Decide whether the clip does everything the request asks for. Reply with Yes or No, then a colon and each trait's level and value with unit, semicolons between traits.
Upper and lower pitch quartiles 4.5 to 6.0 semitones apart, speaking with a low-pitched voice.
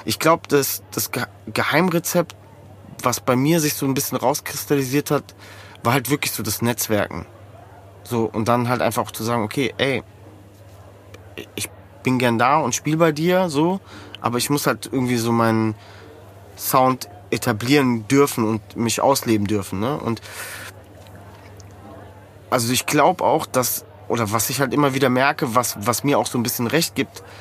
Yes: average, 5.1 semitones; low, 115 Hz